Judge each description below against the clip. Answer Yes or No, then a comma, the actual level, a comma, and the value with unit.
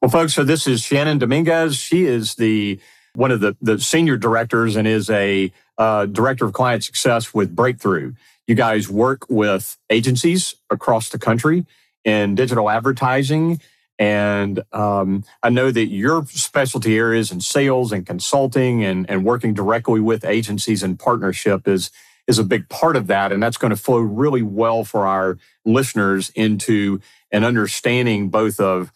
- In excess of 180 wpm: No, average, 165 wpm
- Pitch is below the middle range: Yes, low, 115 Hz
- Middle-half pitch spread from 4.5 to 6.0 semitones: No, average, 3.8 semitones